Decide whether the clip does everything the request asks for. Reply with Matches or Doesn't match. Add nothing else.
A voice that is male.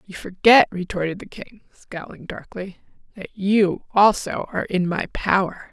Doesn't match